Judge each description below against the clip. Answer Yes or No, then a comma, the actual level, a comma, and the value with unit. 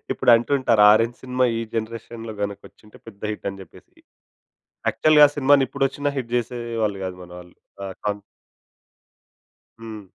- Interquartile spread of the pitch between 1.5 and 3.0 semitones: No, average, 3.6 semitones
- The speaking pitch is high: No, low, 115 Hz